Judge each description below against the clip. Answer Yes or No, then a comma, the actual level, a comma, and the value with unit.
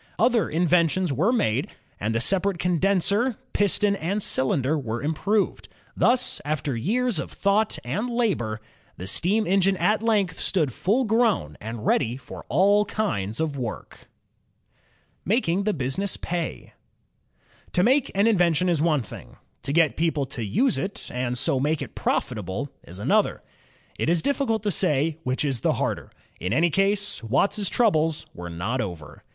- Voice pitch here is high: No, medium, 170 Hz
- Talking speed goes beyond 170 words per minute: No, average, 155 wpm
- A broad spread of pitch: Yes, wide, 7.7 semitones